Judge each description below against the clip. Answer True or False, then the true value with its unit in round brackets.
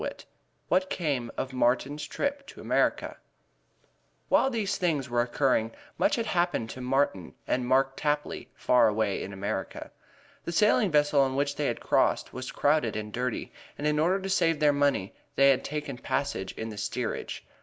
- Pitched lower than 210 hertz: True (140 Hz)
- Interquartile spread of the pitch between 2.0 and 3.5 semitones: False (4.1 semitones)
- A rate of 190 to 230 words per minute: False (170 wpm)